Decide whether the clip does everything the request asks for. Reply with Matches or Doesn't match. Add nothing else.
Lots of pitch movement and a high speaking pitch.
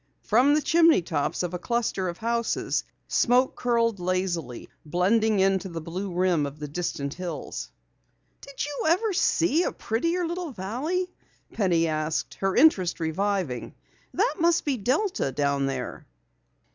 Matches